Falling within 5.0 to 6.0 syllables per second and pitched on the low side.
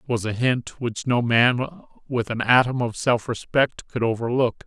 No: 4.7 syllables/s; low, 120 Hz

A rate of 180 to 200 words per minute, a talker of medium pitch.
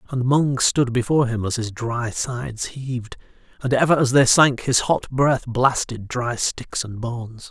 No: average, 185 wpm; low, 125 Hz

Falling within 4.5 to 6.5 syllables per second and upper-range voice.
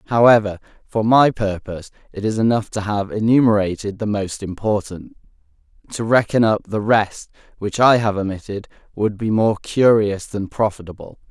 No: 5.0 syllables/s; low, 105 Hz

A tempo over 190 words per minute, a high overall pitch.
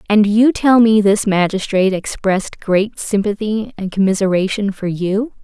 No: average, 145 wpm; high, 205 Hz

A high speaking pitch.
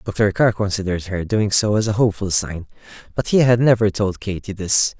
No: low, 100 Hz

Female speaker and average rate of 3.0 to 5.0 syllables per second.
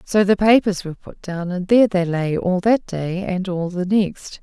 Yes: female; 4.6 syllables/s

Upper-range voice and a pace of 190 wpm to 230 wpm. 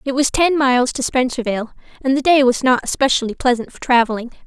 Yes: very high, 255 Hz; average, 200 wpm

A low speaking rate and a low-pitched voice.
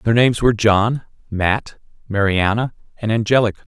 Yes: slow, 130 wpm; low, 110 Hz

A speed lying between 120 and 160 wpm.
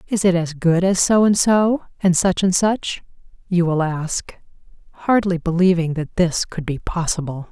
No: average, 175 wpm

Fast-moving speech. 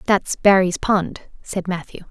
No: average, 140 wpm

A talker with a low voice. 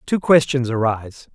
Yes: low, 130 Hz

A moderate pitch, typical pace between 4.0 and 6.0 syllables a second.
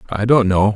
No: low, 105 Hz; 5.9 syllables/s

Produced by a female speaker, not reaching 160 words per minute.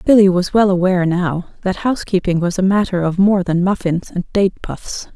No: female; average, 200 wpm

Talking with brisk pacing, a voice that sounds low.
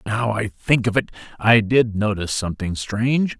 No: average, 175 wpm; low, 110 Hz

